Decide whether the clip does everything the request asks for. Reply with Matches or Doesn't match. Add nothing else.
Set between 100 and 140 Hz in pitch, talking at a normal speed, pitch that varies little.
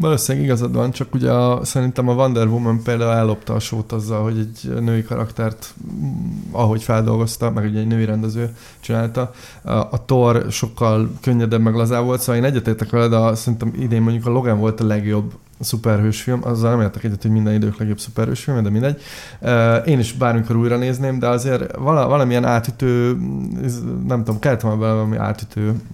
Doesn't match